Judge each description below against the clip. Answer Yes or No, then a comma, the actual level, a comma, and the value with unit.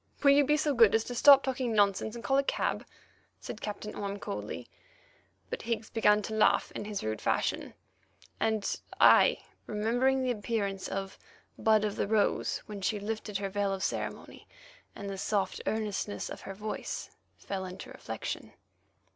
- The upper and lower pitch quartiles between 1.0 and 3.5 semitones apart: Yes, average, 2.7 semitones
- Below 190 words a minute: Yes, average, 170 wpm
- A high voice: Yes, high, 215 Hz